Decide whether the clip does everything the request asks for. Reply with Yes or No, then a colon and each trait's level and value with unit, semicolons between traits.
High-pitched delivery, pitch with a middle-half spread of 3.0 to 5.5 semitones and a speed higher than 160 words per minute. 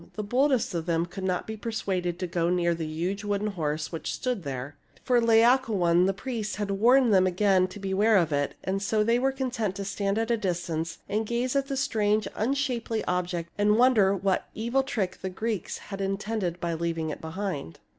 Yes: high, 200 Hz; average, 4.4 semitones; fast, 205 wpm